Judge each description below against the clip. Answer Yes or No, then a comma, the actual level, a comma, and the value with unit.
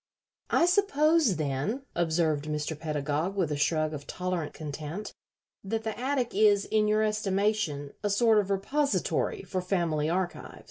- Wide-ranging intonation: Yes, wide, 5.9 semitones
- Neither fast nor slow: Yes, average, 145 wpm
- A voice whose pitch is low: No, high, 190 Hz